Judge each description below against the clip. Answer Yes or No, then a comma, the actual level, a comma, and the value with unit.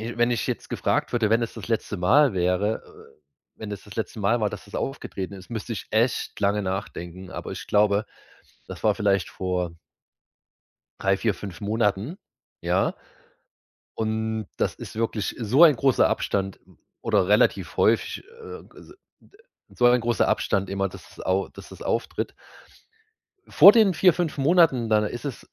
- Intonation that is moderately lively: Yes, average, 3.6 semitones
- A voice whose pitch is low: Yes, low, 110 Hz